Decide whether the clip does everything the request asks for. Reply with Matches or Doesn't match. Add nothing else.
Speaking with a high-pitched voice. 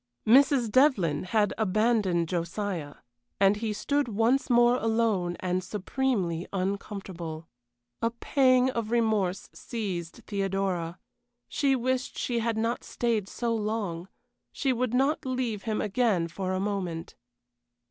Matches